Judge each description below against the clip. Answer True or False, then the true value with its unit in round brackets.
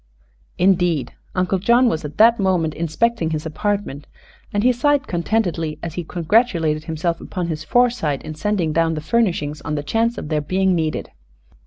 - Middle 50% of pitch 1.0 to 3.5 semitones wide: False (5.2 semitones)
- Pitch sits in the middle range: True (170 Hz)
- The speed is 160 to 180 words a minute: True (170 wpm)